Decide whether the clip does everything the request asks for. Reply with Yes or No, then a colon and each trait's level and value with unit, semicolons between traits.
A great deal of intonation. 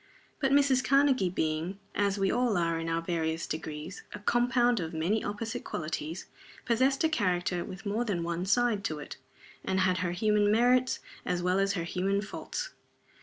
Yes: wide, 5.8 semitones